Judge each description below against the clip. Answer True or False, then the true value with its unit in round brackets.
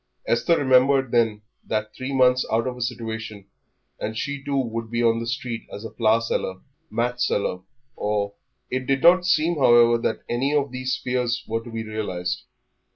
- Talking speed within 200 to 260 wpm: False (180 wpm)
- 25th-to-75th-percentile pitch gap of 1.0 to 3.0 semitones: True (2.5 semitones)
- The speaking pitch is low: True (120 Hz)